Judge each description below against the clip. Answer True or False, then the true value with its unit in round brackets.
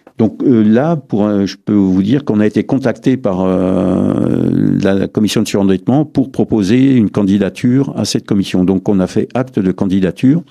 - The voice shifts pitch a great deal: False (4.5 semitones)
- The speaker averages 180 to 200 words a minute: True (190 wpm)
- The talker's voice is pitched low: True (105 Hz)